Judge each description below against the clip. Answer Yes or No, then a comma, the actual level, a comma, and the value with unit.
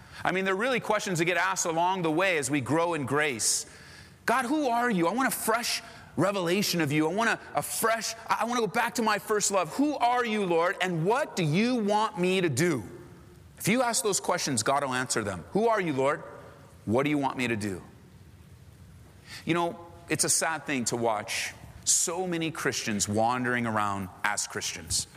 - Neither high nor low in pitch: Yes, medium, 175 Hz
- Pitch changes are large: Yes, wide, 8.1 semitones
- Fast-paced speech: Yes, fast, 210 wpm